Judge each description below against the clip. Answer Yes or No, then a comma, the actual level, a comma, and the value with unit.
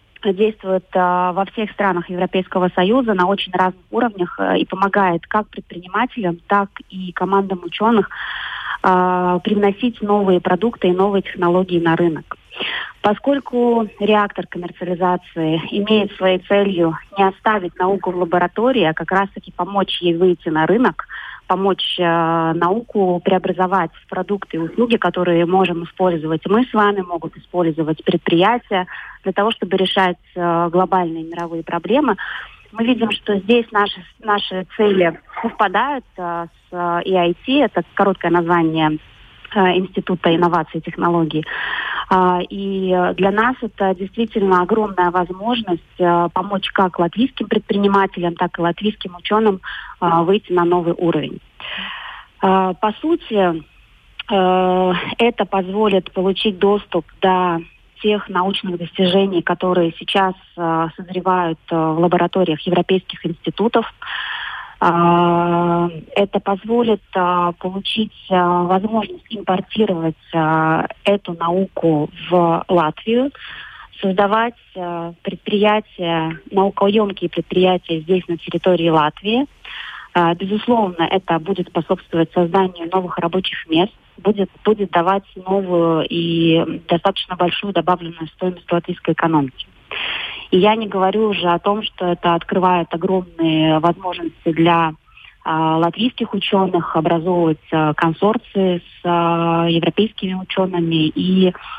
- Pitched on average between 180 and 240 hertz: Yes, medium, 185 Hz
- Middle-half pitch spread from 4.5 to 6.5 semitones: No, average, 2.7 semitones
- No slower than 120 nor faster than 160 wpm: No, slow, 110 wpm